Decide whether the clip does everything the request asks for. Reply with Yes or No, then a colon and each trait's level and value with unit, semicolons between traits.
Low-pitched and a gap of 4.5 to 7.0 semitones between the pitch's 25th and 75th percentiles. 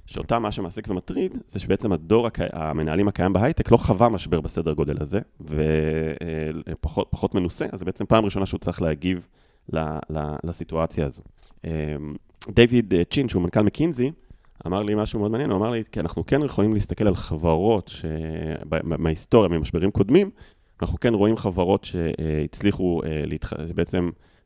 Yes: very low, 90 Hz; average, 4.9 semitones